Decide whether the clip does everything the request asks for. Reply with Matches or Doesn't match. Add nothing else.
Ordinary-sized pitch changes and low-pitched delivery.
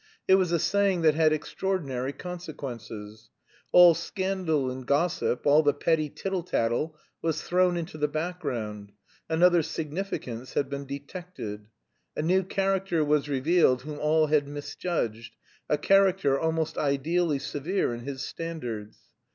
Doesn't match